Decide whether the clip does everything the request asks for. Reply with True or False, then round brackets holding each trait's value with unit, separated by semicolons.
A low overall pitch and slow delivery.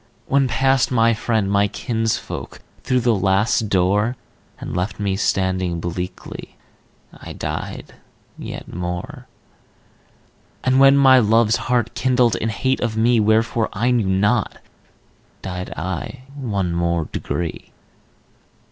True (110 Hz; 120 wpm)